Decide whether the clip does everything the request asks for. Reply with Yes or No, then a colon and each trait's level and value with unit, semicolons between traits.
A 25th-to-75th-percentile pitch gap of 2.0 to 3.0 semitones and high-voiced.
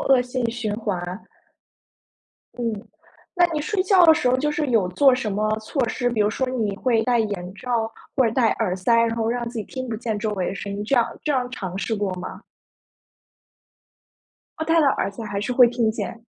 No: average, 3.5 semitones; high, 230 Hz